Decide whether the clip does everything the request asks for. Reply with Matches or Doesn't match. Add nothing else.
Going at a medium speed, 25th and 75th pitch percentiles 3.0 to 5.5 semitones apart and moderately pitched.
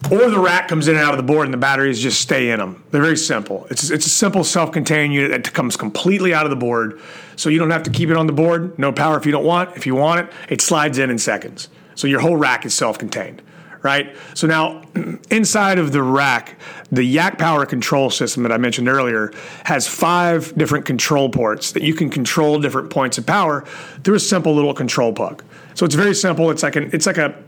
Doesn't match